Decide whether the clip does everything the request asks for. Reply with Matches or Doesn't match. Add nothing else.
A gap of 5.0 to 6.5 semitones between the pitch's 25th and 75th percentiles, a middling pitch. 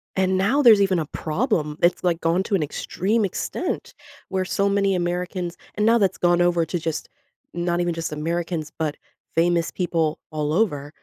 Doesn't match